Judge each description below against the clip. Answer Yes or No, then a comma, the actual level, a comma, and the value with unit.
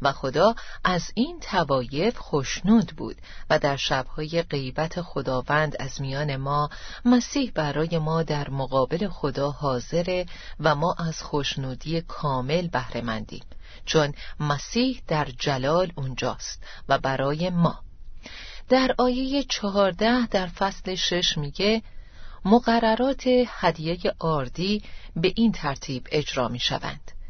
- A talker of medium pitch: Yes, medium, 160 Hz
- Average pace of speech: Yes, average, 115 wpm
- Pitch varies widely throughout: Yes, wide, 5.9 semitones